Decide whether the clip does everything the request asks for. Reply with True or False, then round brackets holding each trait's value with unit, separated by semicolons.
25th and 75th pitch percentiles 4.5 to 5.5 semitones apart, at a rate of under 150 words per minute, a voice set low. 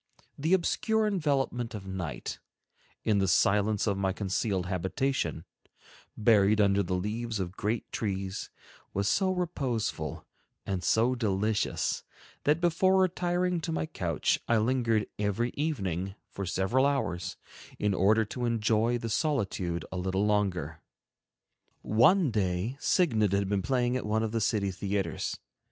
True (5.1 semitones; 140 wpm; 105 Hz)